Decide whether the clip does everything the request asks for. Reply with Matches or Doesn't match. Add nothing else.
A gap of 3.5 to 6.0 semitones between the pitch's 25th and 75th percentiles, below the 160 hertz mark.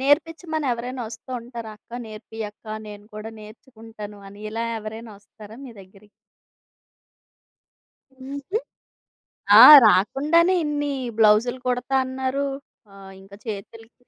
Doesn't match